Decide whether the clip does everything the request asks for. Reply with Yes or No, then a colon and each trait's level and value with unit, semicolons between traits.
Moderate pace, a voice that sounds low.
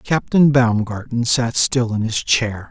Yes: average, 155 wpm; low, 120 Hz